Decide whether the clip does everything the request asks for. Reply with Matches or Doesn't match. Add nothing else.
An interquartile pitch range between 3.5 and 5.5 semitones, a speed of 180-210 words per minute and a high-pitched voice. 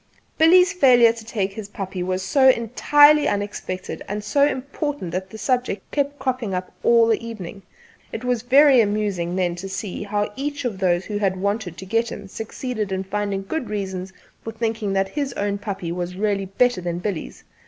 Matches